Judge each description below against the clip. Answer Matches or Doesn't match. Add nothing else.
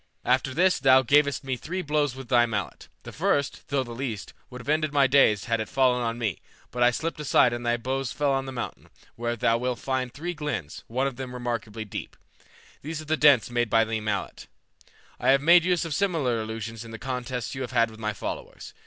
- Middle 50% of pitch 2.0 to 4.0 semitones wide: Matches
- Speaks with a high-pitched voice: Doesn't match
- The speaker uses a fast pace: Matches